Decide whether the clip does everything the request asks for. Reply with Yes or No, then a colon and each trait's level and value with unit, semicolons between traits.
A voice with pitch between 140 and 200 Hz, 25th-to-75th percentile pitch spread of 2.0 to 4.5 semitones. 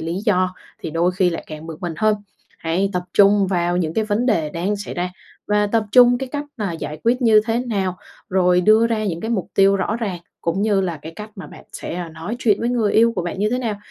Yes: high, 195 Hz; average, 3.9 semitones